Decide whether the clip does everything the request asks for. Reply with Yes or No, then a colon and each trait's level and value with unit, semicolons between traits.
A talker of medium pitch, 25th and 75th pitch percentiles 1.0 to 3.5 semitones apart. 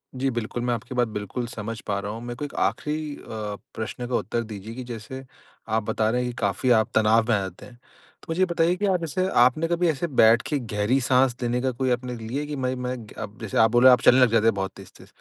No: low, 120 Hz; average, 2.9 semitones